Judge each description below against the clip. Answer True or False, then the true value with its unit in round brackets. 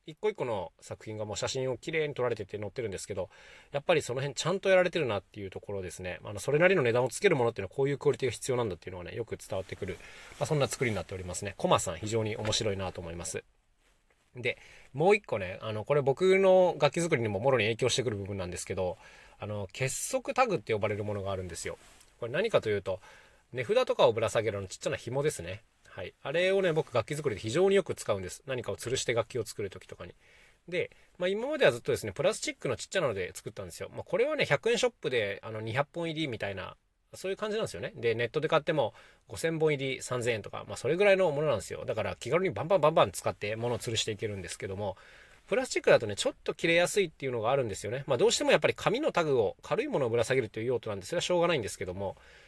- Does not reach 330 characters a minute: False (540 characters per minute)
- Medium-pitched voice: True (145 Hz)